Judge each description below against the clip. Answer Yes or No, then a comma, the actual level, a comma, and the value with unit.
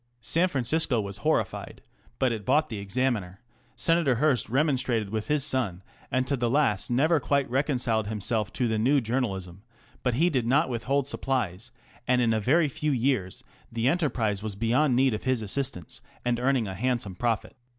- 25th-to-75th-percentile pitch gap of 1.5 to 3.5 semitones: No, average, 4.0 semitones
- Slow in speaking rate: No, average, 175 wpm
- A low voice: Yes, low, 125 Hz